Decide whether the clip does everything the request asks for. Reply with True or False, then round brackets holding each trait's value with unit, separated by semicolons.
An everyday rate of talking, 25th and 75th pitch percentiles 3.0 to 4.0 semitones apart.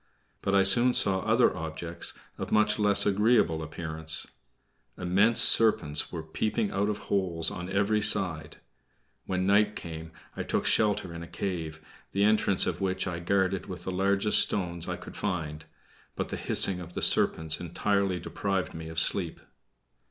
True (160 wpm; 3.5 semitones)